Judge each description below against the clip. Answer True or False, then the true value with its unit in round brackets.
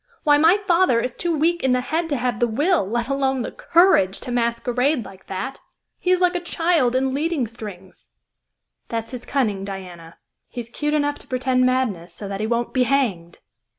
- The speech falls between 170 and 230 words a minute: True (195 wpm)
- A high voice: True (255 Hz)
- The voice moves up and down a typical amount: True (5.0 semitones)